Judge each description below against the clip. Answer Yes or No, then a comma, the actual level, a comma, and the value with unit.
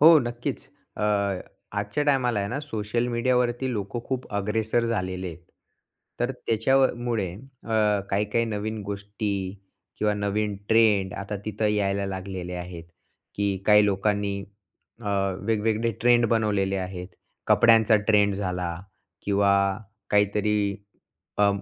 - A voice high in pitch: No, low, 105 Hz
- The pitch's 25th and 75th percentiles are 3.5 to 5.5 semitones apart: No, average, 2.7 semitones